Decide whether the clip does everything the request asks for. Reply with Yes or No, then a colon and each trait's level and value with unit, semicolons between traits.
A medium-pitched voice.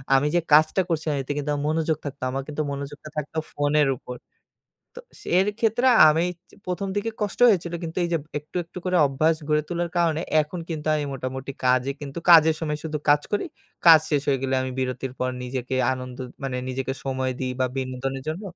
Yes: medium, 150 Hz